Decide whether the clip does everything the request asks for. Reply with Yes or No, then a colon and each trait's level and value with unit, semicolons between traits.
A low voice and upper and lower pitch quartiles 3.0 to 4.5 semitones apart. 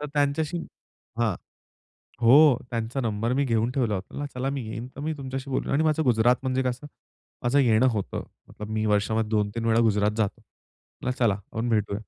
Yes: low, 120 Hz; average, 3.7 semitones